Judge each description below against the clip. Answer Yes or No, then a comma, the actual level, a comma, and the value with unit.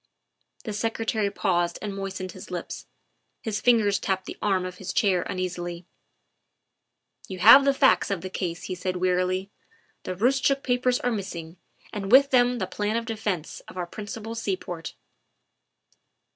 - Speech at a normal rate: Yes, average, 170 wpm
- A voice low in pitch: No, high, 195 Hz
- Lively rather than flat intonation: No, average, 3.8 semitones